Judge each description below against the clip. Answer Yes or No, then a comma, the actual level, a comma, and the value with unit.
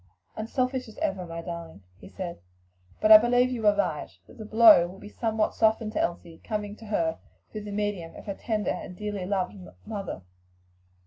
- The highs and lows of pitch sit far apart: No, average, 3.4 semitones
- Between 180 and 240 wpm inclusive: Yes, average, 190 wpm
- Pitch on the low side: No, high, 205 Hz